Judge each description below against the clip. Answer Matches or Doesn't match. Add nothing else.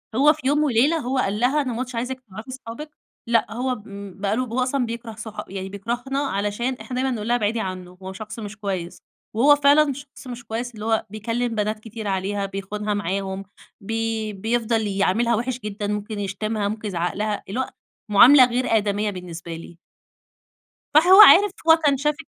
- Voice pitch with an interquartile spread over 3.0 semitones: Matches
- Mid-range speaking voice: Doesn't match